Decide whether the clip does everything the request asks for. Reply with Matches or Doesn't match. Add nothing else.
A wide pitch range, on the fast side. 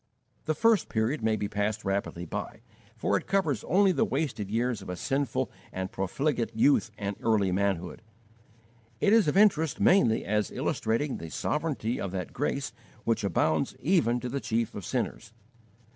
Doesn't match